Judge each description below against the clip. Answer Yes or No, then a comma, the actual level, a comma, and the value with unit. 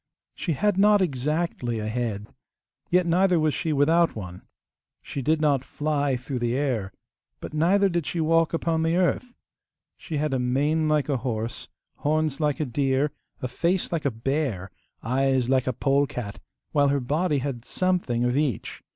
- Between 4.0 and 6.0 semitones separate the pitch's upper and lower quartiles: Yes, average, 4.5 semitones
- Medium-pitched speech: Yes, medium, 145 Hz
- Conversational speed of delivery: Yes, average, 170 wpm